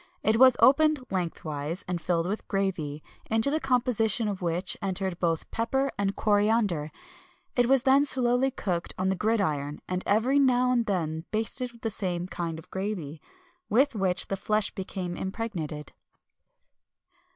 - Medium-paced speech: Yes, average, 155 wpm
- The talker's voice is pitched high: Yes, high, 200 Hz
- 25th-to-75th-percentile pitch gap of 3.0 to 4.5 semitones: No, wide, 5.4 semitones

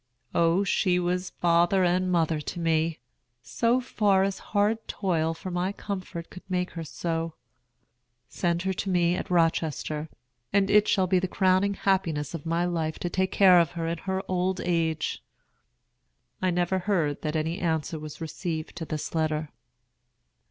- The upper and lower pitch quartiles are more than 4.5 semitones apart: No, narrow, 2.5 semitones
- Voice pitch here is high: No, medium, 175 Hz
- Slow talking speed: No, average, 165 wpm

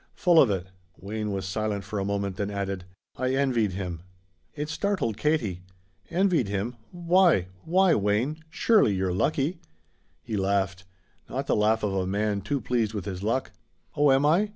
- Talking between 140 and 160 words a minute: No, average, 170 wpm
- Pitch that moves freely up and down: Yes, wide, 7.1 semitones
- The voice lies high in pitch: No, low, 110 Hz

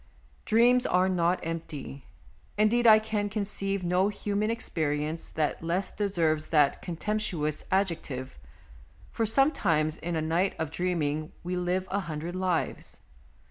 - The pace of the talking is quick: No, slow, 135 wpm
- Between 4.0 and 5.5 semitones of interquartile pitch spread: Yes, average, 4.3 semitones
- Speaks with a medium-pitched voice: Yes, medium, 180 Hz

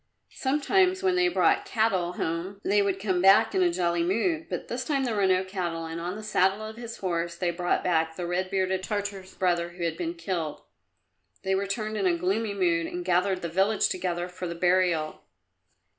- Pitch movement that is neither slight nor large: Yes, average, 3.2 semitones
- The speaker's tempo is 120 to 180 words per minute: No, fast, 205 wpm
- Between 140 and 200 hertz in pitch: Yes, medium, 185 Hz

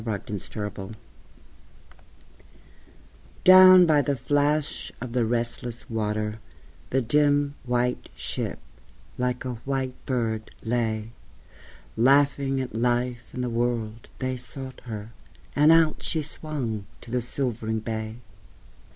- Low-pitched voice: Yes, low, 125 Hz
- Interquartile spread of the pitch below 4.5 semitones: Yes, average, 3.6 semitones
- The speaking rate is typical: No, slow, 120 wpm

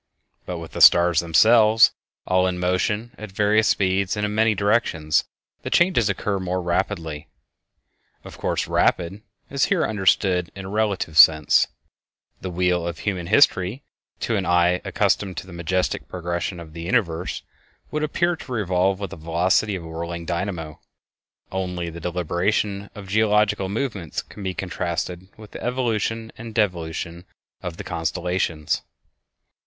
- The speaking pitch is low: Yes, very low, 95 Hz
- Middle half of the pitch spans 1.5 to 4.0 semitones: Yes, average, 3.5 semitones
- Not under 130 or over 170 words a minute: Yes, average, 150 wpm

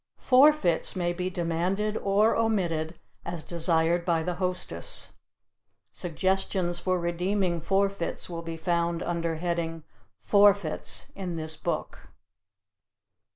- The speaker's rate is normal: No, slow, 110 wpm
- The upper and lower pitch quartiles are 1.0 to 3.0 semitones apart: Yes, narrow, 2.5 semitones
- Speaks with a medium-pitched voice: Yes, medium, 175 Hz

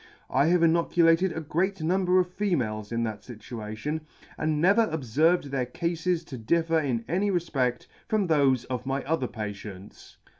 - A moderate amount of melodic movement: No, wide, 5.9 semitones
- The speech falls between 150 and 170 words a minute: Yes, average, 155 wpm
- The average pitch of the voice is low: No, medium, 155 Hz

